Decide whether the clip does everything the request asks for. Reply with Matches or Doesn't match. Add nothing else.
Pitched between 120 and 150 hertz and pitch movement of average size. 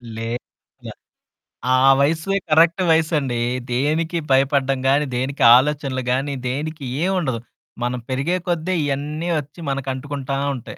Matches